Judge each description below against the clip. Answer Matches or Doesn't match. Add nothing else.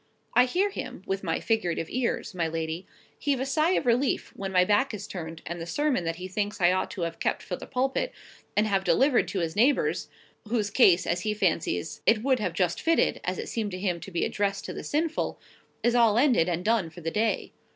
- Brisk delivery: Matches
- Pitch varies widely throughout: Matches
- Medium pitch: Doesn't match